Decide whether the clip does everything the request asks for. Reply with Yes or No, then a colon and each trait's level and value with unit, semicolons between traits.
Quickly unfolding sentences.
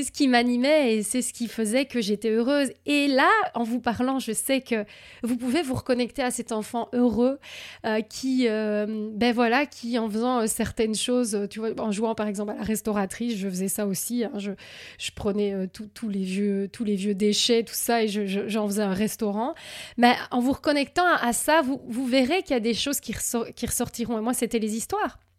Yes: fast, 230 wpm